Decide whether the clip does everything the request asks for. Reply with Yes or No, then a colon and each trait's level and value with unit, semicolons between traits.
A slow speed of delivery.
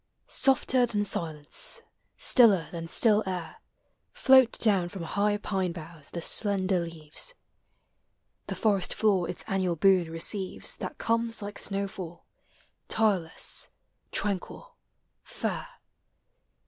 Yes: slow, 110 wpm